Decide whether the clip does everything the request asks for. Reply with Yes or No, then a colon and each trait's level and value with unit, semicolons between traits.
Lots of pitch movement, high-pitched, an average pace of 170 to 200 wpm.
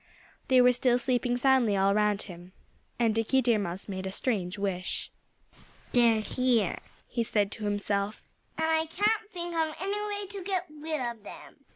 Yes: wide, 6.6 semitones; high, 235 Hz; average, 175 wpm